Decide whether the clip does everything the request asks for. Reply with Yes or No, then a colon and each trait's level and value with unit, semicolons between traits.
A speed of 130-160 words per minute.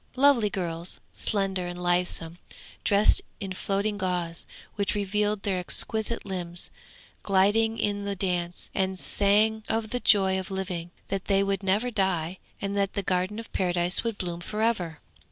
Yes: average, 155 wpm